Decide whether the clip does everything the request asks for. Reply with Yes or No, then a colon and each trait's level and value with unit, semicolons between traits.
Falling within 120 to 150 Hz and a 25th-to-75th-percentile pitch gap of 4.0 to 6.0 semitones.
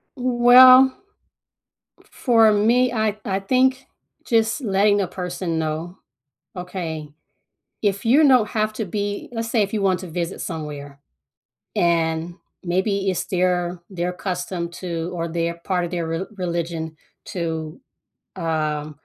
No: medium, 180 Hz; average, 4.3 semitones